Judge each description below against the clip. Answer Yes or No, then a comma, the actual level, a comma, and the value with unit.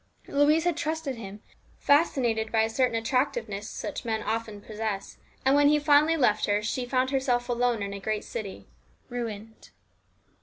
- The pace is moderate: Yes, average, 160 wpm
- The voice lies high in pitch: Yes, high, 235 Hz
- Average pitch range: Yes, average, 4.3 semitones